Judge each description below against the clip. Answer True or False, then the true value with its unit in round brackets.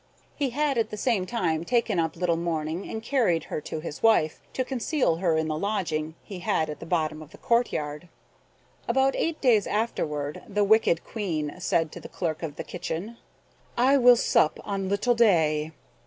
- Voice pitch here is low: False (180 Hz)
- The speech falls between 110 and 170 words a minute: False (185 wpm)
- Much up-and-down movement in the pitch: True (6.7 semitones)